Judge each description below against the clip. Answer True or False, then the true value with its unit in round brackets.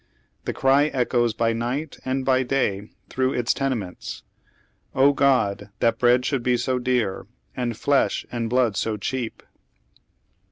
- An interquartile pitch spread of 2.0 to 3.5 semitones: True (2.5 semitones)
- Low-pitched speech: True (125 Hz)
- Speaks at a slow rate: False (150 wpm)